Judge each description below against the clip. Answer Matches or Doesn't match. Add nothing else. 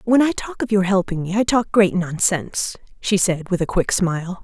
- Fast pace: Matches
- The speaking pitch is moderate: Doesn't match